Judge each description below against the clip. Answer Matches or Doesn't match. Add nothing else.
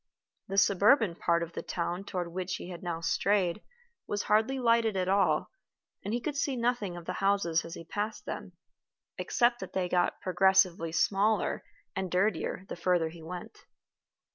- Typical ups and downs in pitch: Matches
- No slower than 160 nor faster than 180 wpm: Matches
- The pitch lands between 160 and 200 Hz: Matches